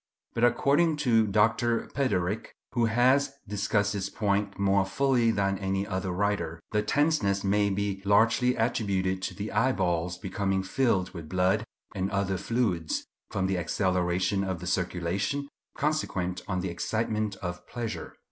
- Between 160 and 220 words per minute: No, average, 145 wpm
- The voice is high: No, low, 100 Hz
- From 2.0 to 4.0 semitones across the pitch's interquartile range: Yes, average, 3.4 semitones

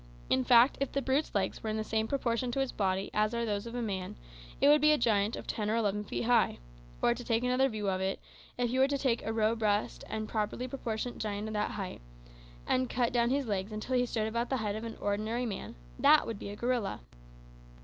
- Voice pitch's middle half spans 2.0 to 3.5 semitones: Yes, average, 2.9 semitones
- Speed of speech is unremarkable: No, fast, 240 wpm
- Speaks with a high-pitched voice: Yes, high, 225 Hz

